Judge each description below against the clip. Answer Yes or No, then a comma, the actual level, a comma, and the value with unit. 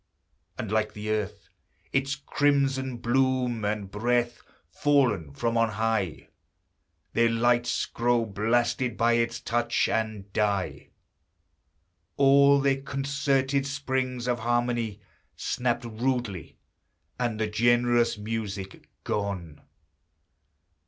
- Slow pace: Yes, slow, 100 wpm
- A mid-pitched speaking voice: No, low, 120 Hz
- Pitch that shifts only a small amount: No, average, 3.3 semitones